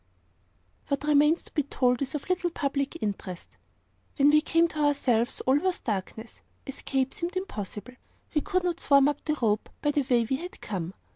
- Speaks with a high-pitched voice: Yes, very high, 280 Hz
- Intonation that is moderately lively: Yes, average, 4.0 semitones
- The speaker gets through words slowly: No, average, 185 wpm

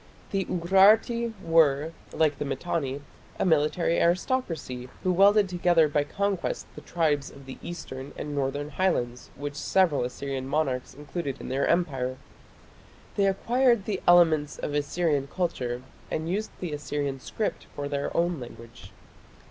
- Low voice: No, medium, 155 Hz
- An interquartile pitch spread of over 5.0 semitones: No, average, 4.5 semitones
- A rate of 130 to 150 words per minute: Yes, average, 140 wpm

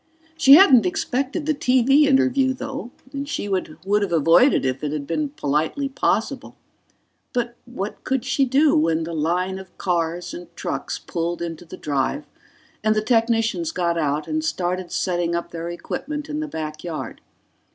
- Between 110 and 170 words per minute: Yes, average, 165 wpm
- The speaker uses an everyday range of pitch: No, wide, 8.2 semitones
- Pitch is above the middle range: Yes, high, 195 Hz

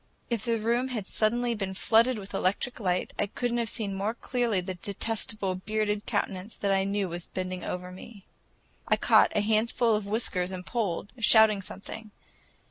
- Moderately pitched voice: No, high, 210 Hz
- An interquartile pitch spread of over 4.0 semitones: No, average, 3.0 semitones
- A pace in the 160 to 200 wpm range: Yes, average, 180 wpm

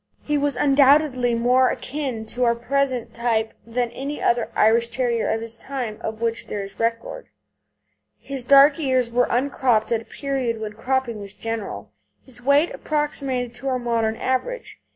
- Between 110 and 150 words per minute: No, average, 165 wpm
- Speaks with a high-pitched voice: Yes, high, 245 Hz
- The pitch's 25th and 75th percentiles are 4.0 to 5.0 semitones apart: No, average, 3.0 semitones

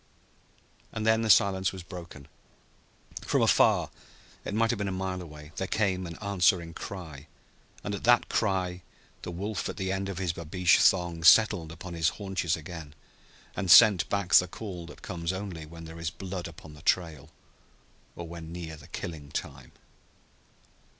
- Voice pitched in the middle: No, very low, 90 Hz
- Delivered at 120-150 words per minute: No, average, 170 wpm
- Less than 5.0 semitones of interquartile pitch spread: Yes, average, 2.8 semitones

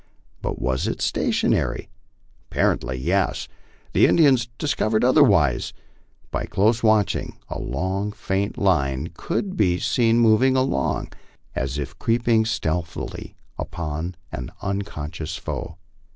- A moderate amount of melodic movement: No, wide, 6.6 semitones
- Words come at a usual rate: No, slow, 110 wpm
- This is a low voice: Yes, low, 100 Hz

